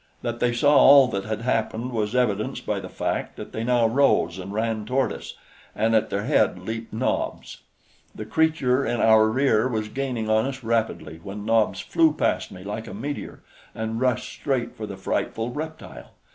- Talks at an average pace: Yes, average, 185 wpm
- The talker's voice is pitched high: No, low, 115 Hz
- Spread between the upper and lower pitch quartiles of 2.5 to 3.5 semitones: Yes, average, 2.9 semitones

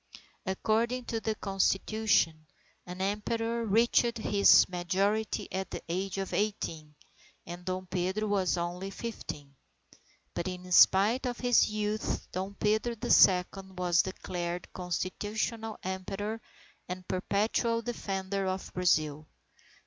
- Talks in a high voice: Yes, high, 195 Hz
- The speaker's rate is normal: No, slow, 120 wpm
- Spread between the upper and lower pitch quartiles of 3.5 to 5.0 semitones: No, average, 3.1 semitones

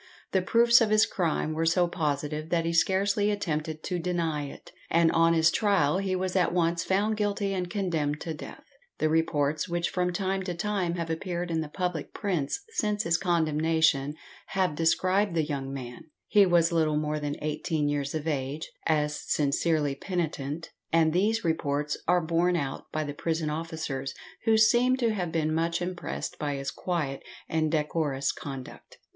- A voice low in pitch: No, medium, 165 Hz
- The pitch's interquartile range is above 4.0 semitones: No, average, 3.4 semitones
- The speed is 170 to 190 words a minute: Yes, average, 175 wpm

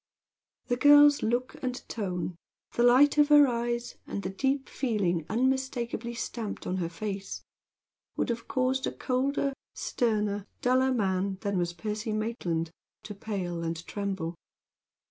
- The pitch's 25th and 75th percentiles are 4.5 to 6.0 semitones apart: Yes, average, 4.9 semitones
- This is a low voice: No, high, 225 Hz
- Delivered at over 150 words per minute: No, average, 145 wpm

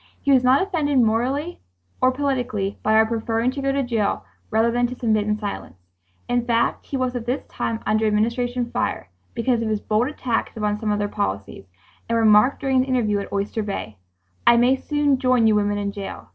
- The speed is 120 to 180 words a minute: No, fast, 205 wpm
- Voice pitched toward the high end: Yes, high, 230 Hz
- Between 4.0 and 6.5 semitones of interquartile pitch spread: No, average, 3.3 semitones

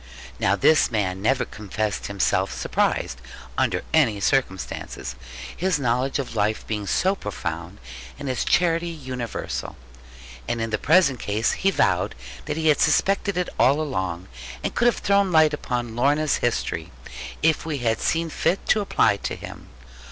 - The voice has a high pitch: No, low, 130 Hz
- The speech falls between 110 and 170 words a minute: Yes, average, 155 wpm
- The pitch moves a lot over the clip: Yes, wide, 7.2 semitones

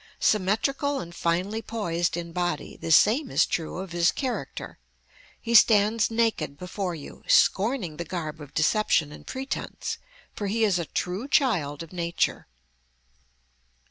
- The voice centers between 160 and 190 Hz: Yes, medium, 185 Hz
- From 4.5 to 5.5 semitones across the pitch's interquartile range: Yes, average, 5.0 semitones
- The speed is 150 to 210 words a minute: No, average, 140 wpm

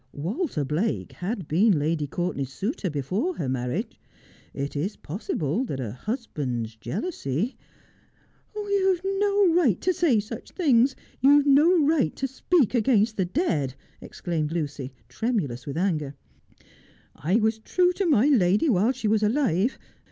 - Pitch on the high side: Yes, high, 210 Hz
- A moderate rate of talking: Yes, average, 160 wpm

